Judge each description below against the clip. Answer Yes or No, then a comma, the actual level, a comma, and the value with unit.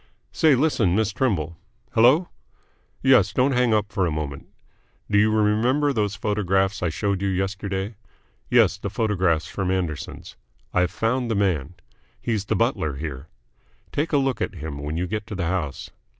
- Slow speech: No, average, 165 wpm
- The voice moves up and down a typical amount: Yes, average, 4.3 semitones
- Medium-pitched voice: No, low, 100 Hz